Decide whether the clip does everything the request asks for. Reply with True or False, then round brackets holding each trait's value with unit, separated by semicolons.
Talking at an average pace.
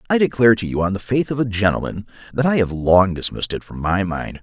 False (260 wpm)